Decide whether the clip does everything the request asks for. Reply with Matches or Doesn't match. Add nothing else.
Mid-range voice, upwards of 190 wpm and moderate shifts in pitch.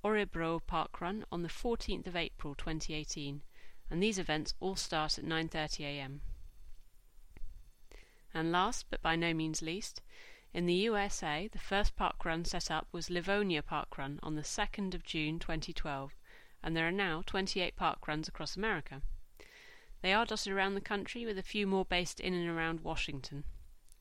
Doesn't match